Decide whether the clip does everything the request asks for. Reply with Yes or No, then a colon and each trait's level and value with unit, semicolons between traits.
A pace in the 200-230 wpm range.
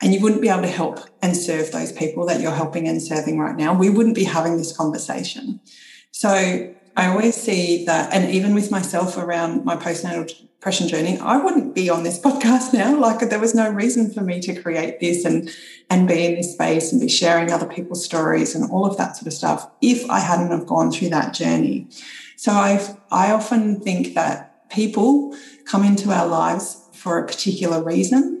Yes: fast, 205 wpm